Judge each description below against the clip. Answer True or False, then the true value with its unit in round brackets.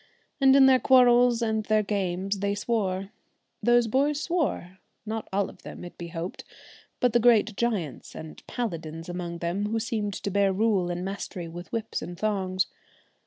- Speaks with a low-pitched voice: False (205 Hz)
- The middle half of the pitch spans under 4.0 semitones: False (4.4 semitones)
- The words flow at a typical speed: True (170 wpm)